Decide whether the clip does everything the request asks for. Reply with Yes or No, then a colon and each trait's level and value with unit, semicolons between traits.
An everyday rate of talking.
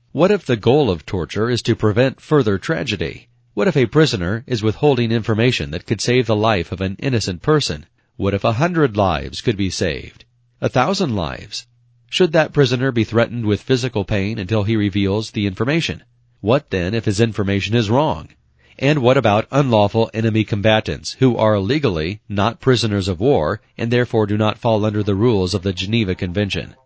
Yes: average, 185 wpm